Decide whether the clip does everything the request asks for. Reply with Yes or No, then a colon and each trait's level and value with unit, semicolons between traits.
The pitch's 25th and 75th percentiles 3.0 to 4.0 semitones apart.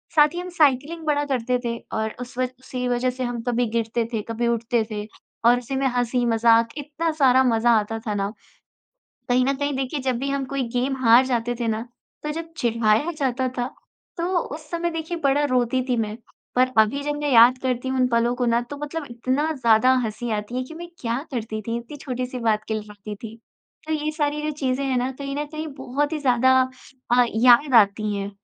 Yes: average, 3.5 semitones